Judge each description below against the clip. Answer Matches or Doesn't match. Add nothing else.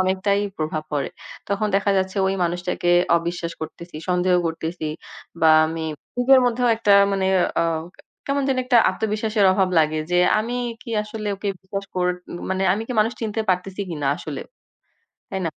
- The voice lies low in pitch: Doesn't match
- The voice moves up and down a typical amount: Matches